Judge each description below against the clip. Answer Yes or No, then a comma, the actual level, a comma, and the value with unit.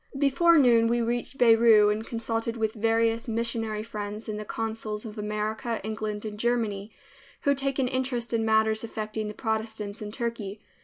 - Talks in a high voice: Yes, high, 225 Hz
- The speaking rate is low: No, average, 165 wpm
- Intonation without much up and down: Yes, narrow, 1.6 semitones